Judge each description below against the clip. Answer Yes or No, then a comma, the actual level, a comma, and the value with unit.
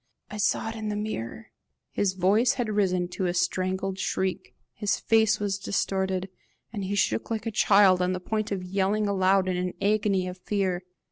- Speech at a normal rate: Yes, average, 190 wpm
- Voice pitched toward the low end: No, high, 195 Hz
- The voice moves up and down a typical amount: No, narrow, 2.2 semitones